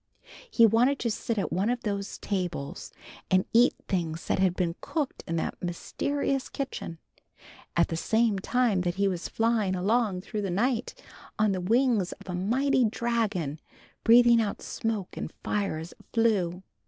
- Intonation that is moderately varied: Yes, average, 4.5 semitones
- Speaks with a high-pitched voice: Yes, high, 205 Hz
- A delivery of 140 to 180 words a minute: Yes, average, 165 wpm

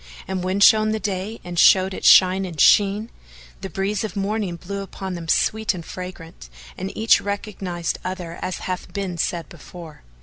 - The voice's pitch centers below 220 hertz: Yes, high, 190 Hz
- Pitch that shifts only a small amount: Yes, narrow, 2.3 semitones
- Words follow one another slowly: No, average, 175 wpm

